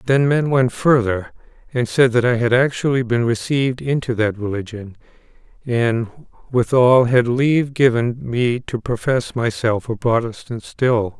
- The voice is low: Yes, low, 120 Hz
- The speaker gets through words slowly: No, average, 145 wpm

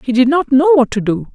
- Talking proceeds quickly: Yes, fast, 310 wpm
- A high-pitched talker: Yes, very high, 260 Hz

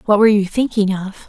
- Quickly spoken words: Yes, fast, 235 wpm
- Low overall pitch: No, high, 205 Hz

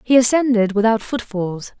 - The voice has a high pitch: Yes, high, 225 Hz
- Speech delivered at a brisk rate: No, slow, 135 wpm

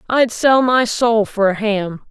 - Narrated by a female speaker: Yes, female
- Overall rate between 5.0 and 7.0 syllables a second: No, 3.8 syllables/s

